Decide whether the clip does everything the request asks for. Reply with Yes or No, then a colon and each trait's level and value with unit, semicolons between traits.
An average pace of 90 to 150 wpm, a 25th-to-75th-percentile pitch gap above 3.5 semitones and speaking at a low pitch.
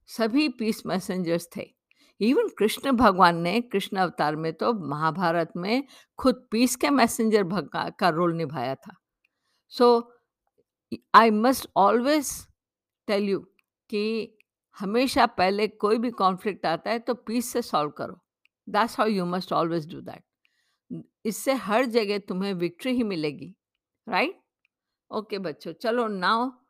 No: average, 135 wpm; average, 4.8 semitones; high, 215 Hz